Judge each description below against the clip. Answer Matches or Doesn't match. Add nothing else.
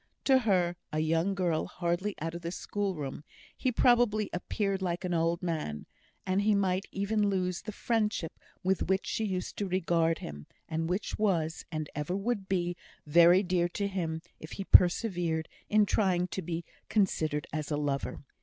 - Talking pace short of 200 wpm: Matches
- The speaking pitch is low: Doesn't match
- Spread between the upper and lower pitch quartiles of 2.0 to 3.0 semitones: Doesn't match